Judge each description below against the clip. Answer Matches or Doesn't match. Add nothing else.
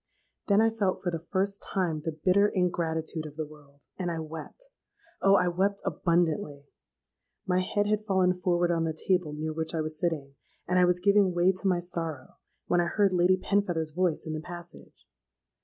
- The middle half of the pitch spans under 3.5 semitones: Matches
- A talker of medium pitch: Matches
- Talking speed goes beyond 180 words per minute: Matches